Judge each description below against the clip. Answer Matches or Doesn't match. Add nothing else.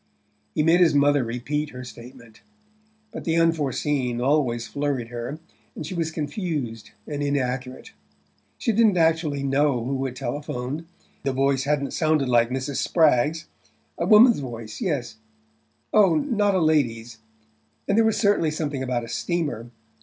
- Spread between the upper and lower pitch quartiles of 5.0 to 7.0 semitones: Doesn't match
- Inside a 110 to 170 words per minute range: Matches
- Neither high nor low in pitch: Matches